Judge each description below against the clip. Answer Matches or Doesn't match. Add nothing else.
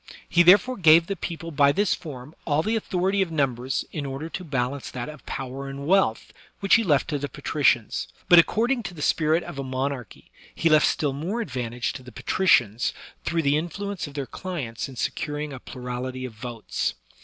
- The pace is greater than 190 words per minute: Matches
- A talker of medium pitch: Matches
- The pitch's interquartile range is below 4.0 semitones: Doesn't match